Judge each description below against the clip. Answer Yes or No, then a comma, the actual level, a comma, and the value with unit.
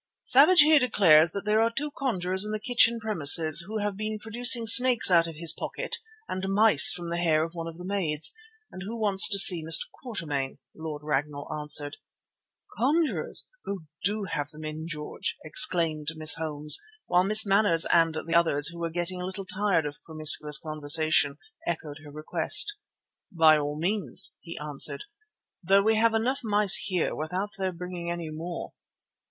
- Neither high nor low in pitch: Yes, medium, 175 Hz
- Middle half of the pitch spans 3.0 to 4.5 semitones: No, average, 5.2 semitones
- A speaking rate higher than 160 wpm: Yes, average, 175 wpm